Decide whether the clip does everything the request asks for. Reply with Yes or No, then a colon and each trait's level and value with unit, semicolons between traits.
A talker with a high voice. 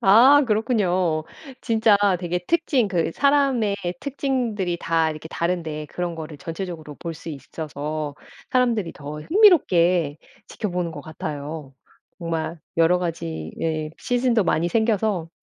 No: medium, 175 Hz